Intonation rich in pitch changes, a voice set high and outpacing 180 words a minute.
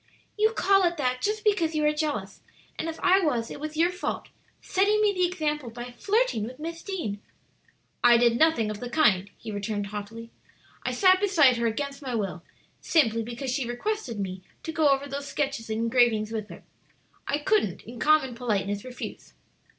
Yes: wide, 6.4 semitones; very high, 265 Hz; average, 190 wpm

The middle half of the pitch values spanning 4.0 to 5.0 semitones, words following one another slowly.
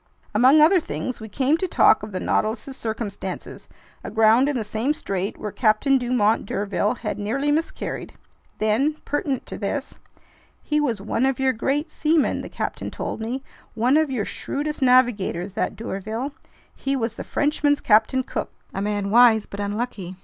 No: average, 4.5 semitones; average, 165 wpm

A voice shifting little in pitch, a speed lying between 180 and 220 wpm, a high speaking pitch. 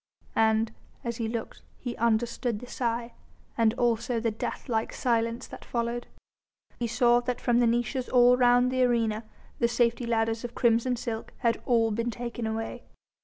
No: narrow, 1.1 semitones; average, 170 wpm; high, 235 Hz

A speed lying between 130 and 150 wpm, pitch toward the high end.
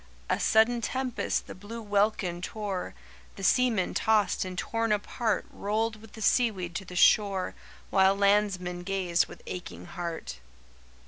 Yes: average, 140 wpm; high, 200 Hz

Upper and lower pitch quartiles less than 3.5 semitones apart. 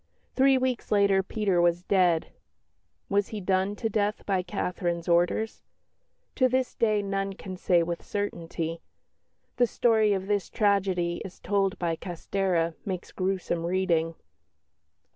Yes: average, 2.9 semitones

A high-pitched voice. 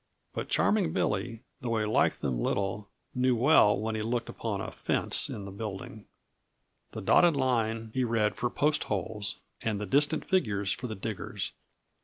No: low, 110 Hz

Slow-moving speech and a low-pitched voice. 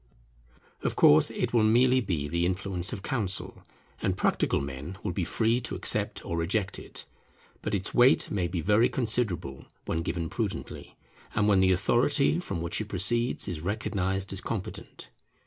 No: average, 165 wpm; very low, 95 Hz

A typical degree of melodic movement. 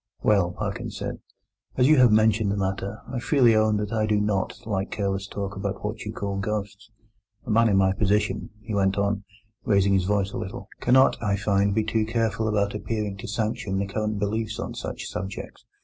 No: narrow, 1.8 semitones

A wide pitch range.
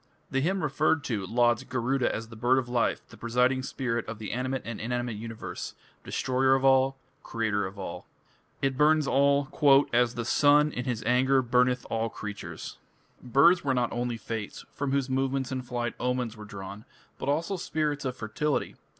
No: average, 2.8 semitones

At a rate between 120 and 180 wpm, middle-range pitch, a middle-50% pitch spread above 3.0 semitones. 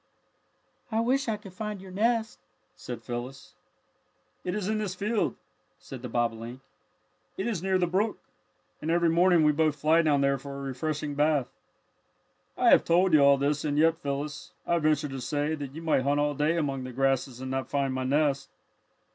No: average, 190 wpm; medium, 150 Hz; average, 4.5 semitones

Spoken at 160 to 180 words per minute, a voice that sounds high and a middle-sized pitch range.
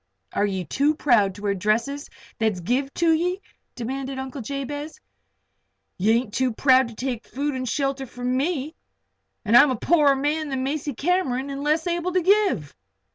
Yes: average, 175 wpm; very high, 270 Hz; average, 3.8 semitones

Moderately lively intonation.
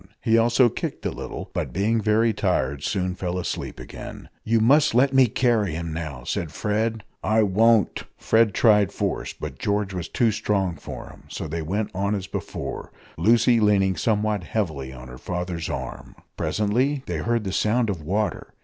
Yes: average, 4.2 semitones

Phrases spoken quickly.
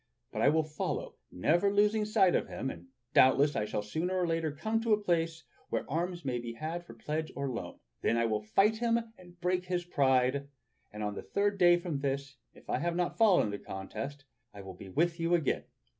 Yes: fast, 220 wpm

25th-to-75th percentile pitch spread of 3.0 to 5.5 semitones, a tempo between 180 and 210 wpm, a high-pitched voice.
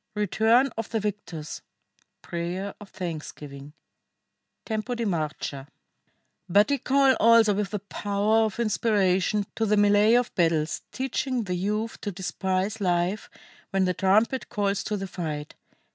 No: average, 3.5 semitones; average, 140 wpm; high, 205 Hz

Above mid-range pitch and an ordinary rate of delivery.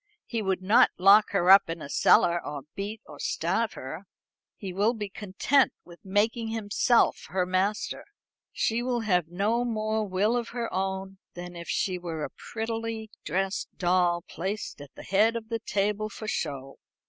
Yes: high, 200 Hz; average, 170 wpm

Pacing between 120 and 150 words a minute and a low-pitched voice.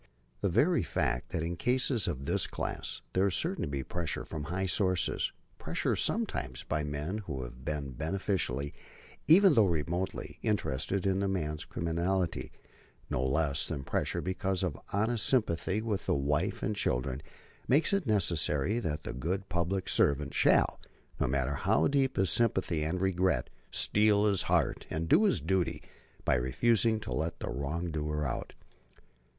No: average, 160 wpm; very low, 85 Hz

